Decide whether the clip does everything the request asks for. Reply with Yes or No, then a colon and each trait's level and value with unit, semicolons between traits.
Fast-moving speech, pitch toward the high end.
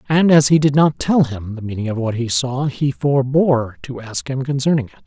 No: fast, 235 wpm; low, 135 Hz